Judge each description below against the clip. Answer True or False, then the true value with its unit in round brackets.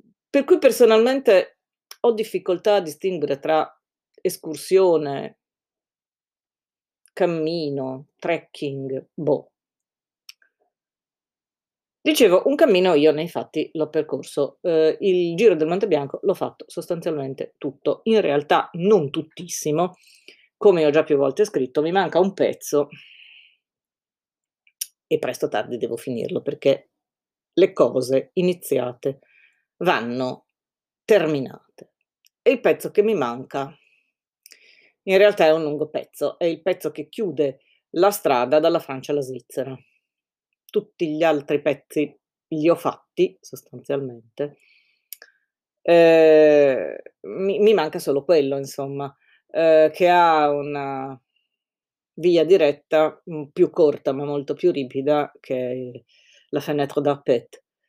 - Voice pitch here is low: False (155 Hz)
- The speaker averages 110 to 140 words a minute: True (115 wpm)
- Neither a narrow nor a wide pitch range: True (4.9 semitones)